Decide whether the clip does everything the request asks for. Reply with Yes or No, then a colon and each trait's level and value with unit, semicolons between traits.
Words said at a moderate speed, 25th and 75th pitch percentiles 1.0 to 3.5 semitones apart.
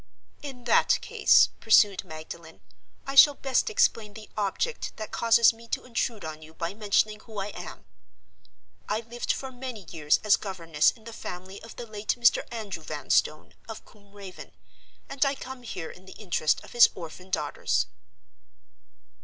No: average, 165 wpm; average, 4.4 semitones